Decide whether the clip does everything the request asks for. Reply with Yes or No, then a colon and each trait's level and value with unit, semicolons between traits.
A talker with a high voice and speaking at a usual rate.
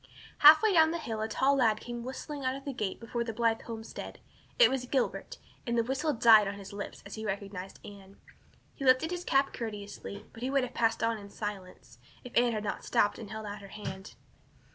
No: high, 230 Hz; fast, 220 wpm